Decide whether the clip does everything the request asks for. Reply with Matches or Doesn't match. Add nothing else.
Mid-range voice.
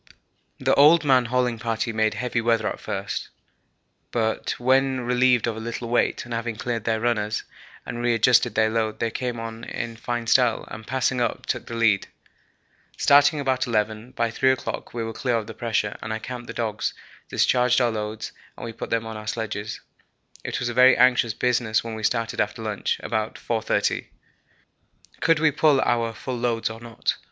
Doesn't match